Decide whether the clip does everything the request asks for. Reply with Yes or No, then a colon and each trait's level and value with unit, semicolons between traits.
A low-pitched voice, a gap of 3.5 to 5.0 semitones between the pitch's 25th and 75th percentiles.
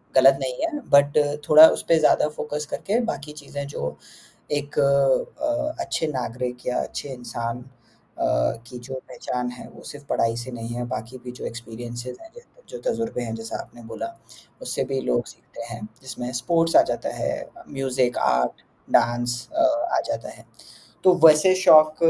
Yes: low, 130 Hz; average, 4.0 semitones